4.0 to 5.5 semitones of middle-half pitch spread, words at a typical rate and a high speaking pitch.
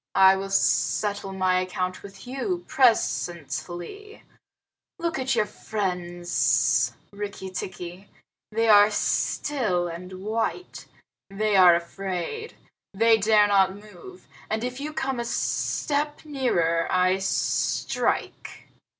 No: average, 4.6 semitones; slow, 110 wpm; high, 195 Hz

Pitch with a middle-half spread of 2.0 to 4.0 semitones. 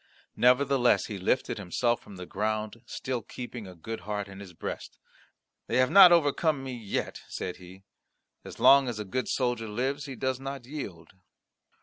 No: average, 4.7 semitones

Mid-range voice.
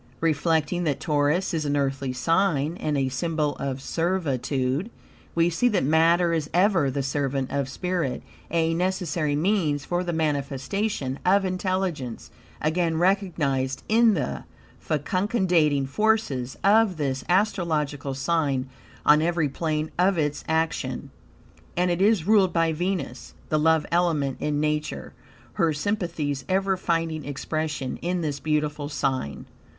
Yes: medium, 160 Hz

